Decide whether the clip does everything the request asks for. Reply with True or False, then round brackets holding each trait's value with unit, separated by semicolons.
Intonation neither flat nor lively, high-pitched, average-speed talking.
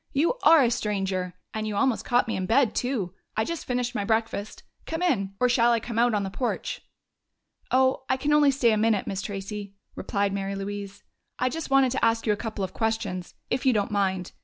False (4.0 semitones; 225 Hz; 220 wpm)